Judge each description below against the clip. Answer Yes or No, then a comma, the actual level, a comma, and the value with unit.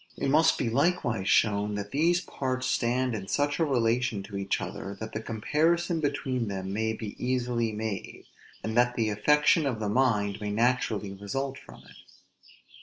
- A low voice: Yes, low, 115 Hz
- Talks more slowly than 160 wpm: No, average, 175 wpm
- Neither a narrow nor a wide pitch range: Yes, average, 4.4 semitones